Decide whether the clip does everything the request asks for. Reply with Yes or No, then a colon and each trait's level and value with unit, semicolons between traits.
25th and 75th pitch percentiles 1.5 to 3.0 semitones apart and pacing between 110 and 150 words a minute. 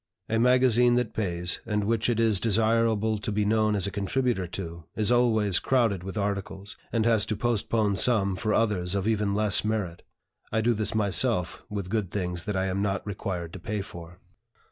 No: average, 2.7 semitones; average, 190 wpm